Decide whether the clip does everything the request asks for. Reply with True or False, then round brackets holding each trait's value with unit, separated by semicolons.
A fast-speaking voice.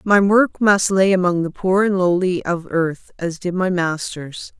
False (195 wpm)